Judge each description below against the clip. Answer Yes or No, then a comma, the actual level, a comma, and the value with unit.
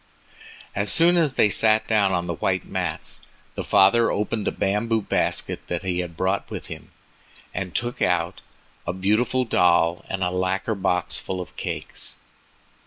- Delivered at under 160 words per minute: No, average, 175 wpm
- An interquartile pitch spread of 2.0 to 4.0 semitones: Yes, average, 3.6 semitones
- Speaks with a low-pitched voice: Yes, very low, 95 Hz